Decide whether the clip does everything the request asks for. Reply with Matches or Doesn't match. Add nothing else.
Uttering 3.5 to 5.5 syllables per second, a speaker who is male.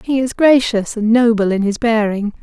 Doesn't match